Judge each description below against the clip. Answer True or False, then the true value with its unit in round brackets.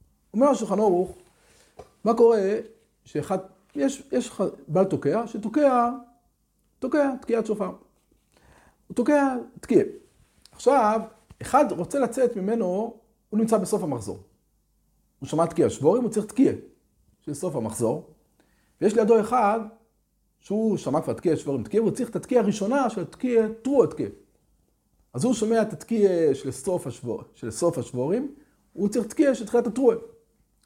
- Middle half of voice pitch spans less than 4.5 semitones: False (5.0 semitones)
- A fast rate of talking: False (135 wpm)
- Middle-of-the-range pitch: False (220 Hz)